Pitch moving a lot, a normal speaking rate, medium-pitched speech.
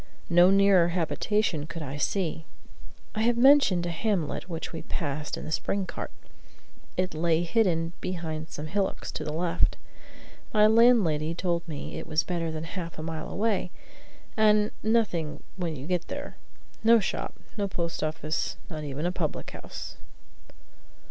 No: average, 4.0 semitones; average, 155 wpm; medium, 170 Hz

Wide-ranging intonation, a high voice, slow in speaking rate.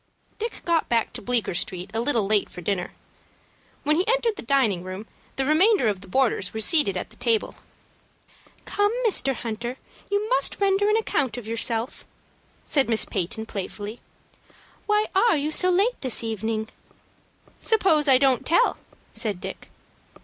No: wide, 8.9 semitones; very high, 250 Hz; average, 155 wpm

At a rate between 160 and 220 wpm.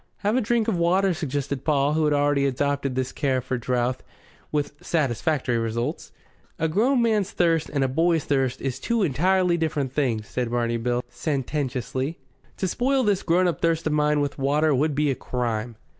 Yes: average, 185 wpm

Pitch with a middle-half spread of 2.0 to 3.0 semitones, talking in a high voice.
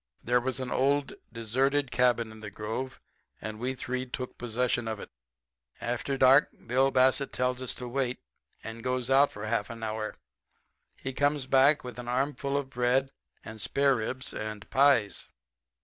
No: narrow, 2.6 semitones; low, 125 Hz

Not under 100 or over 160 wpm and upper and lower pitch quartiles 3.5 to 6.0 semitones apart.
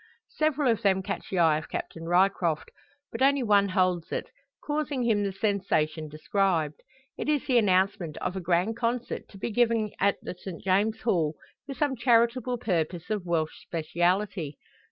No: average, 170 wpm; average, 5.1 semitones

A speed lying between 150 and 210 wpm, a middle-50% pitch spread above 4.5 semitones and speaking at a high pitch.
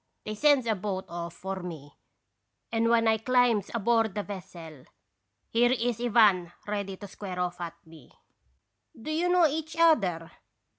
Yes: average, 160 wpm; average, 4.9 semitones; high, 210 Hz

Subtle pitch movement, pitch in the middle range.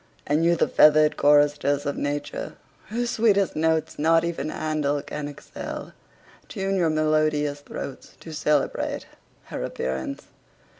Yes: narrow, 2.1 semitones; medium, 155 Hz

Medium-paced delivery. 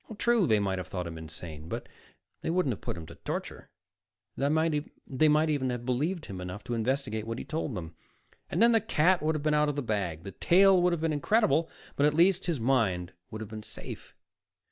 No: fast, 220 wpm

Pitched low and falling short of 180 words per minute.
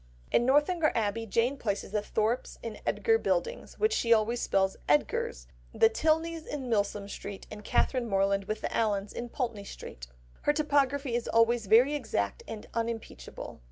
No: high, 230 Hz; average, 160 wpm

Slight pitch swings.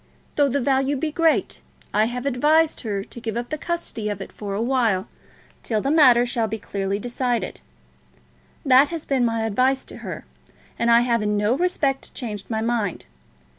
No: average, 3.8 semitones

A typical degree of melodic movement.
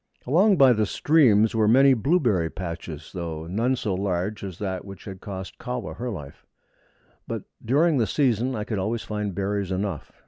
Yes: average, 4.8 semitones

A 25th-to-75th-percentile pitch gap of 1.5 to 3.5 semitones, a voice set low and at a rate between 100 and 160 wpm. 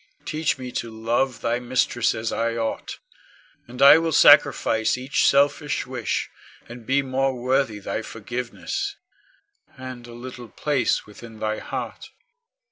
Yes: narrow, 2.5 semitones; low, 125 Hz; slow, 135 wpm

